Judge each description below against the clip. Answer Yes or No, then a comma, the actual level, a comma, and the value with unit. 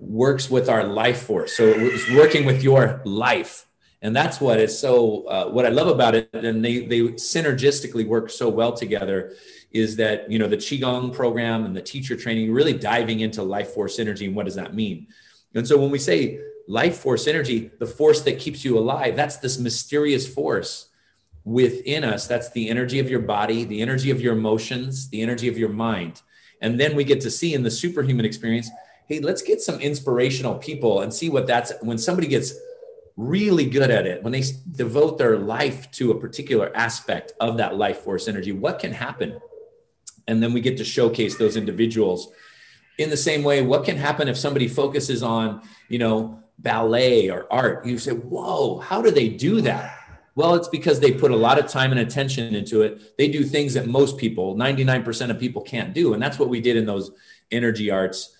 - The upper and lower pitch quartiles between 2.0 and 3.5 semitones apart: No, average, 4.2 semitones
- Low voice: Yes, low, 125 Hz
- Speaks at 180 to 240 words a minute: Yes, average, 200 wpm